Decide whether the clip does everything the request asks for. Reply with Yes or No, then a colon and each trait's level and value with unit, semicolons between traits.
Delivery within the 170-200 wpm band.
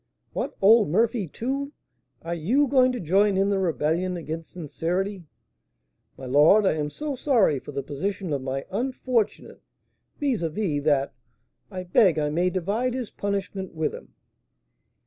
No: average, 155 wpm